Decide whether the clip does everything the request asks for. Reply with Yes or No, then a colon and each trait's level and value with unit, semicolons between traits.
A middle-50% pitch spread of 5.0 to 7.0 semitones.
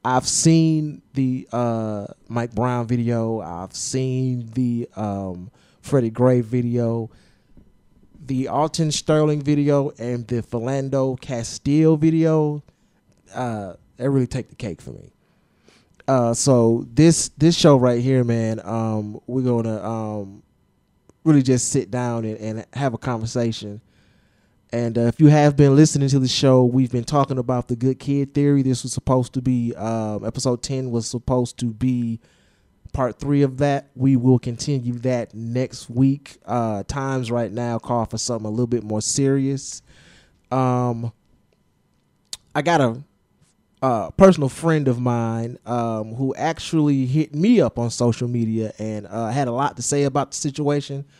No: average, 3.2 semitones